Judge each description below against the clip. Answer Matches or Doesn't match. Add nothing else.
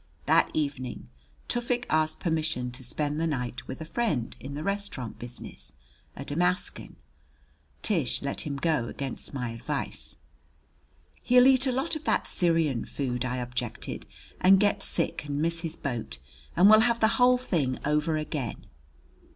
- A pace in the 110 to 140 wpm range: Doesn't match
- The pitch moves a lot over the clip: Matches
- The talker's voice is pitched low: Doesn't match